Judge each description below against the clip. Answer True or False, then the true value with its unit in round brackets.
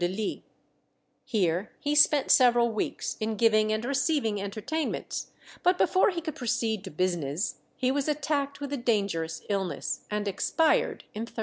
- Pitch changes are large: True (6.0 semitones)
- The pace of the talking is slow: False (145 wpm)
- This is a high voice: True (225 Hz)